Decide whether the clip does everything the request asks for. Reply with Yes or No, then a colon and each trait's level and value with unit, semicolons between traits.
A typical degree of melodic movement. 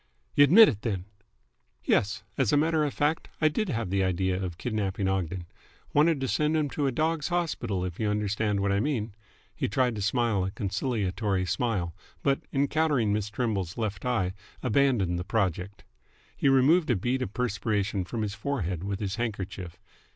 No: wide, 5.9 semitones